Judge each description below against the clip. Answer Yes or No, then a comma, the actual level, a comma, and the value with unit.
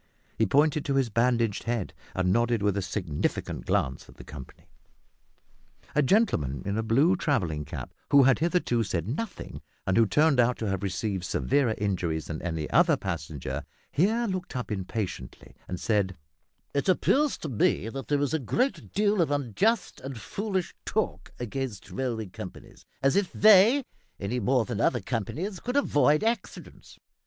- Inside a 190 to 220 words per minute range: No, average, 165 wpm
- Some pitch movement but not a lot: No, wide, 8.3 semitones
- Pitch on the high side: No, low, 120 Hz